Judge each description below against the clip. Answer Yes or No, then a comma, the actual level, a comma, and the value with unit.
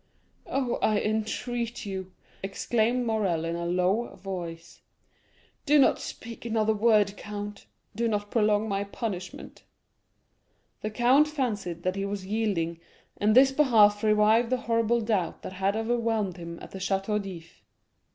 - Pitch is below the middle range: No, high, 210 Hz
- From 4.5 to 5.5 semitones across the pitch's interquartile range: No, average, 3.1 semitones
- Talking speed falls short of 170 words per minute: Yes, average, 140 wpm